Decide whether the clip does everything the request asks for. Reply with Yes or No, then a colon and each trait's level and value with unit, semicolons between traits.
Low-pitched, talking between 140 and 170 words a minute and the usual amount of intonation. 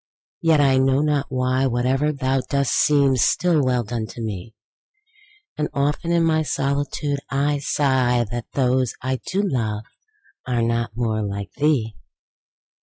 Yes: low, 130 Hz; average, 150 wpm; average, 3.2 semitones